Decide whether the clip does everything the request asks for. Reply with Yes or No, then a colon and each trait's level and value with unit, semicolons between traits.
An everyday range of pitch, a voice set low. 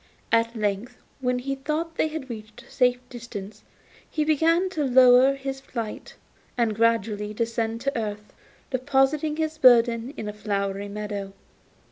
No: average, 4.2 semitones; high, 240 Hz